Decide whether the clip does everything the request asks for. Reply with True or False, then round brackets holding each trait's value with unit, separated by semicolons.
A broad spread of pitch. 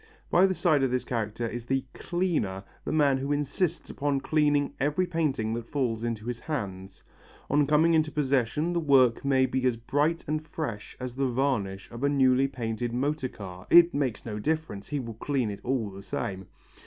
False (4.4 semitones)